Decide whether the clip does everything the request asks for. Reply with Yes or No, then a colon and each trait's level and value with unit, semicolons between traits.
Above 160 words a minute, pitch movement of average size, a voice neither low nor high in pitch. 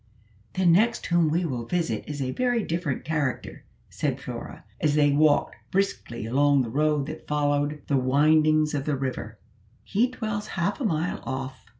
Yes: average, 170 wpm; average, 3.7 semitones; medium, 150 Hz